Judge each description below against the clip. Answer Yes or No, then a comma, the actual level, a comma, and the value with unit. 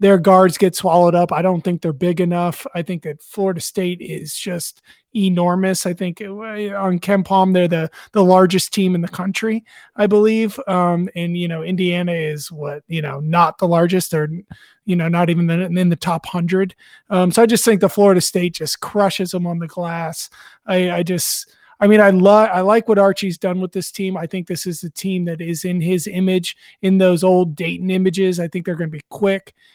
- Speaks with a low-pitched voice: No, medium, 180 Hz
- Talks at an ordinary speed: No, fast, 220 wpm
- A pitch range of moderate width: No, narrow, 2.0 semitones